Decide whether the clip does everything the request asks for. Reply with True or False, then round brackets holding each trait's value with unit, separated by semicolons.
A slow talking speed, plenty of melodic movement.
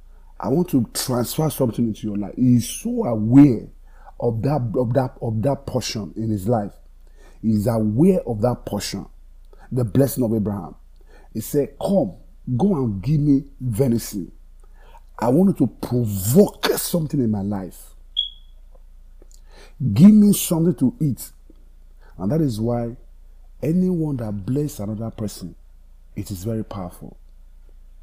False (145 wpm; 7.0 semitones)